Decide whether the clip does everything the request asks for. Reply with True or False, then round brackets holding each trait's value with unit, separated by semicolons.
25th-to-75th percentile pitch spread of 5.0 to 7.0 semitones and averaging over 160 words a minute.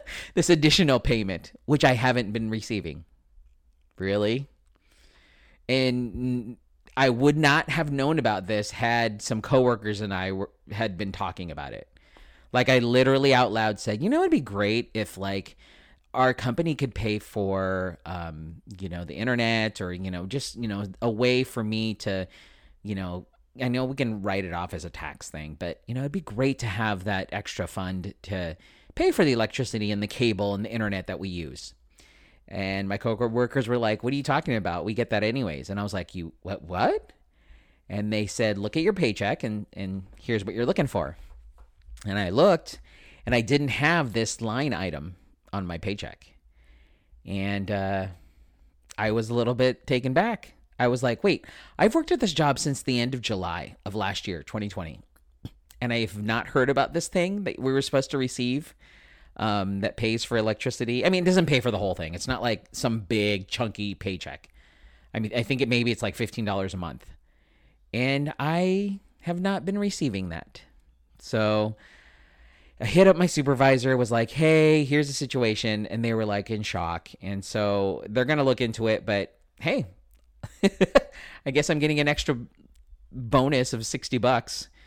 True (5.6 semitones; 185 wpm)